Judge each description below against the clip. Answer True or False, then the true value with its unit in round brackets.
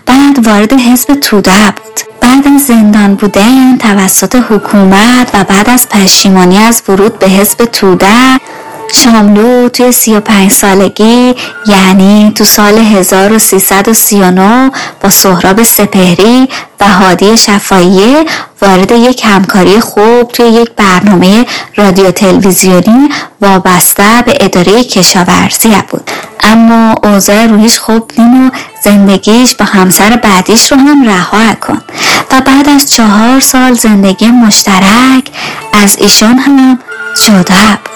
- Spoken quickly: False (115 wpm)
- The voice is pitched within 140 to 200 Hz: False (215 Hz)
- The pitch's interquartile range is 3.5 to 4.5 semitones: True (3.8 semitones)